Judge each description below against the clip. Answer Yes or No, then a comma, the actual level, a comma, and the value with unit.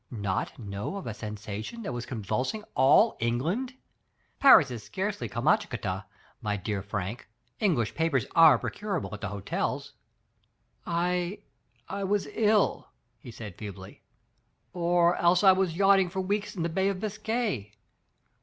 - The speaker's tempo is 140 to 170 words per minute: Yes, average, 145 wpm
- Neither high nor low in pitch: Yes, medium, 165 Hz